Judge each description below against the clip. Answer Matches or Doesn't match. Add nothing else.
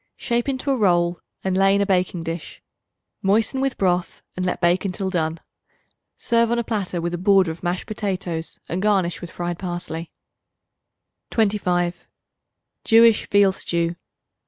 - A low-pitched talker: Doesn't match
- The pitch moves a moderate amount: Matches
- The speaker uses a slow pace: Doesn't match